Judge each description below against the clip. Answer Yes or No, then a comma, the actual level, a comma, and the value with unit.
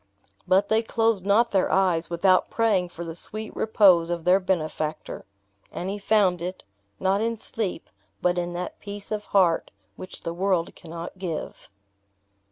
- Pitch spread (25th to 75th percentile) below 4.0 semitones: Yes, average, 2.9 semitones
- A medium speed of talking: Yes, average, 160 wpm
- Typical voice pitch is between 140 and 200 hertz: Yes, medium, 185 Hz